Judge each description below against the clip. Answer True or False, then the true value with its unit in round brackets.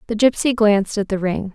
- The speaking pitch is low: False (215 Hz)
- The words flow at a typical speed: False (235 wpm)